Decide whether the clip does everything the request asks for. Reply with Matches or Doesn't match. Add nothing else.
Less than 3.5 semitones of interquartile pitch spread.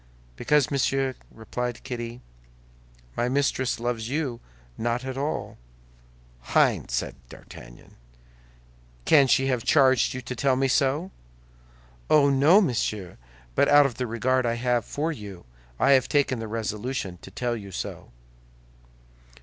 Matches